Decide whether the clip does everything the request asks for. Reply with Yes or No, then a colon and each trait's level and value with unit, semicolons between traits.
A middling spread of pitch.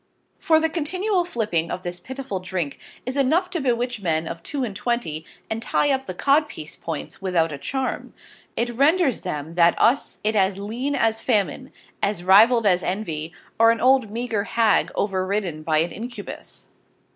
No: wide, 6.6 semitones